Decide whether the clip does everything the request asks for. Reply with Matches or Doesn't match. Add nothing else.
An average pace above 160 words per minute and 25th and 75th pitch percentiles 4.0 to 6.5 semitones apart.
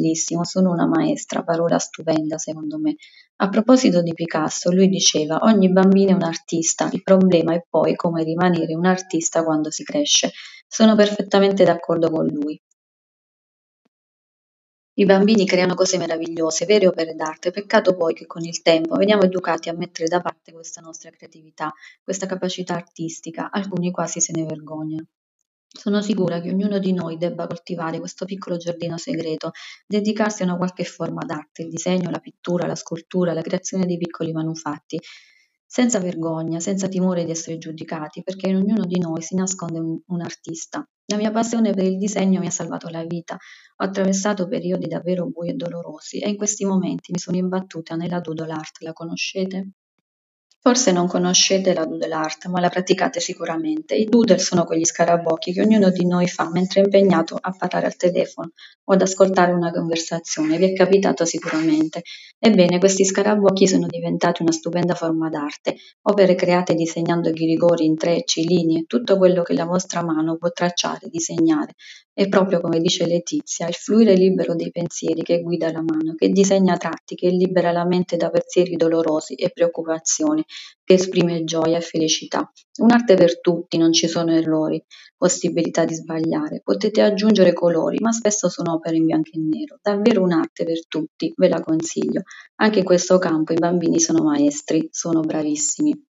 Doesn't match